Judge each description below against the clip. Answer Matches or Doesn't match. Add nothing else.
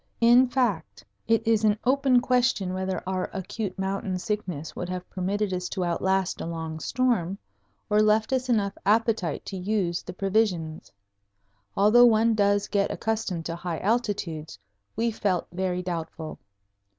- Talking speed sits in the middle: Matches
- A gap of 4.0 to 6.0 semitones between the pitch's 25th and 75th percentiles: Doesn't match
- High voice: Matches